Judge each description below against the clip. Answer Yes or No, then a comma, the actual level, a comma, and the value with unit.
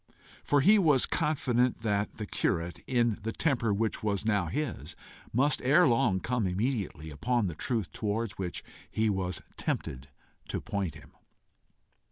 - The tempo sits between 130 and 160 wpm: Yes, average, 150 wpm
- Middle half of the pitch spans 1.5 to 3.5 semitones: No, average, 4.6 semitones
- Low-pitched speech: Yes, low, 110 Hz